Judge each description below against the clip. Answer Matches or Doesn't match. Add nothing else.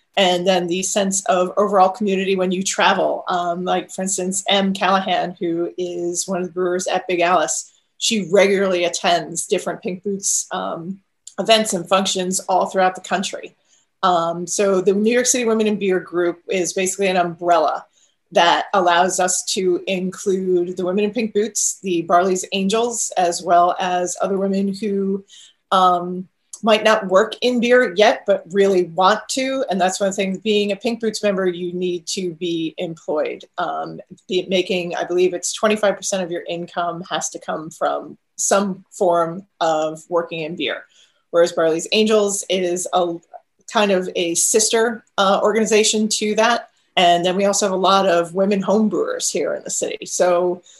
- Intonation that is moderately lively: Doesn't match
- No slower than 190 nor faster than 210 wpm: Doesn't match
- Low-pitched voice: Doesn't match